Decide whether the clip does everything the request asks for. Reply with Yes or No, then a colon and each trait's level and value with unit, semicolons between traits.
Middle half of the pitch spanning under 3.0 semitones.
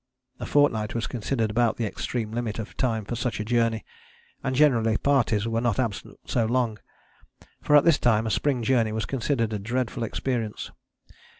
Yes: narrow, 2.5 semitones